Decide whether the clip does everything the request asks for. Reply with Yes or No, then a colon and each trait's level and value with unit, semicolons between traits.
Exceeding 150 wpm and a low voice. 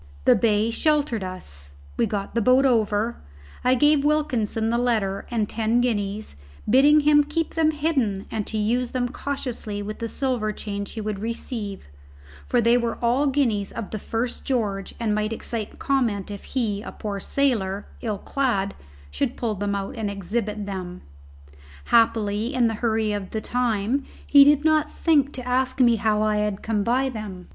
No: average, 175 wpm; high, 225 Hz